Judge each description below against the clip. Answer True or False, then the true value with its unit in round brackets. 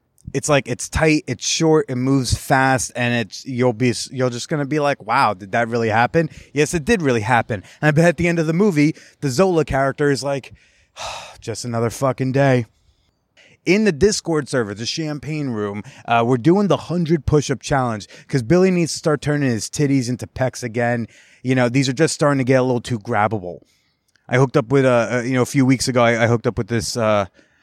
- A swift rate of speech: True (215 wpm)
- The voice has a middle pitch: False (130 Hz)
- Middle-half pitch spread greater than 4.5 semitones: False (3.9 semitones)